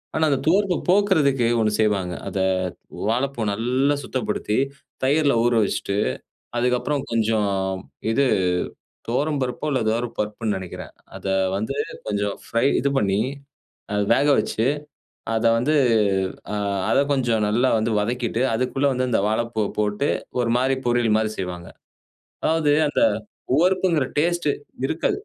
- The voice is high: No, low, 120 Hz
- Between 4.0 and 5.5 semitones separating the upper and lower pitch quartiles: Yes, average, 4.6 semitones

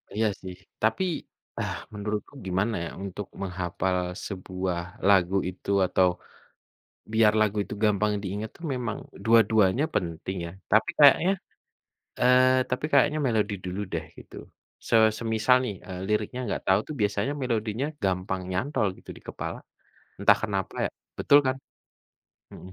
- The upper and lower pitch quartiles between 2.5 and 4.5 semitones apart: Yes, average, 3.5 semitones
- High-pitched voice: No, low, 105 Hz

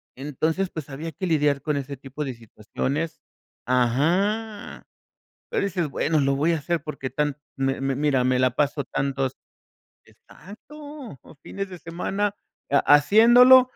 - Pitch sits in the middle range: Yes, medium, 150 Hz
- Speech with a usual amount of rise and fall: No, wide, 5.9 semitones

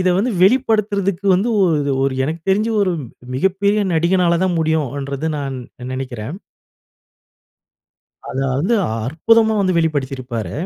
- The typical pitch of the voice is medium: Yes, medium, 170 Hz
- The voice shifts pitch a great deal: Yes, wide, 6.5 semitones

